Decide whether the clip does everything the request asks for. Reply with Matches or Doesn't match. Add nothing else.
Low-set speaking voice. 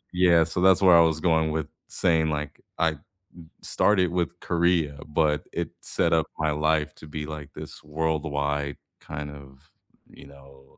Matches